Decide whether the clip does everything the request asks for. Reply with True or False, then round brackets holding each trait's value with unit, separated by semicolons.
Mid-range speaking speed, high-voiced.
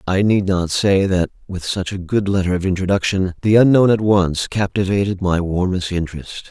False (185 wpm; 95 Hz)